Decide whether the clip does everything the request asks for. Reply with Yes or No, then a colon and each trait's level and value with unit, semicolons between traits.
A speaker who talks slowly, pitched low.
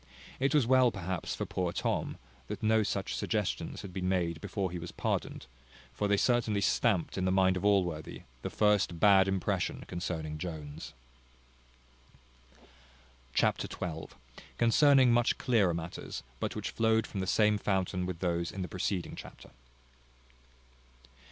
No: average, 145 wpm; very low, 95 Hz